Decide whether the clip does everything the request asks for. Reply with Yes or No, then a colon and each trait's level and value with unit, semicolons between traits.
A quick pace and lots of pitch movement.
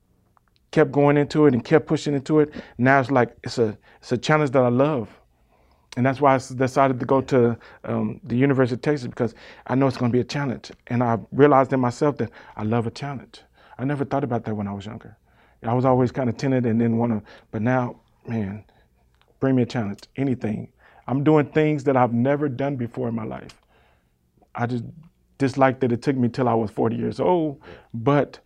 No: fast, 220 wpm; average, 3.3 semitones